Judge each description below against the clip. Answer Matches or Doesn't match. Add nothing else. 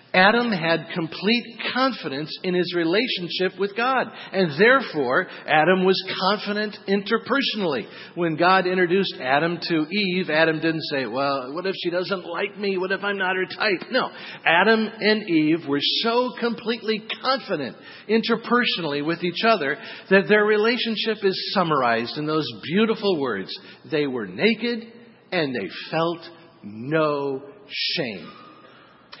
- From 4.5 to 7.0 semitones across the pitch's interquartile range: Matches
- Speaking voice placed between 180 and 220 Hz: Matches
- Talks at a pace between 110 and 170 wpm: Matches